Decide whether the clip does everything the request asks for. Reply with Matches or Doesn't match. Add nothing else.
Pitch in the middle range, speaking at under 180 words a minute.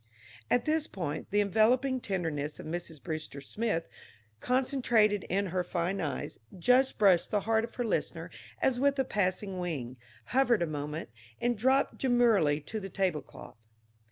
Doesn't match